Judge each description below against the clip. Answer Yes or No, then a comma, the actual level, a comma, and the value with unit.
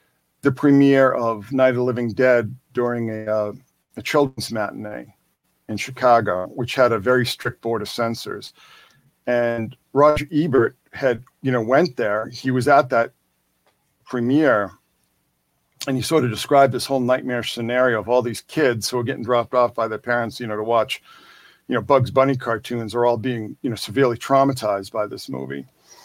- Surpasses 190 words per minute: No, average, 175 wpm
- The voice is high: No, low, 120 Hz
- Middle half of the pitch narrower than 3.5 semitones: Yes, narrow, 2.6 semitones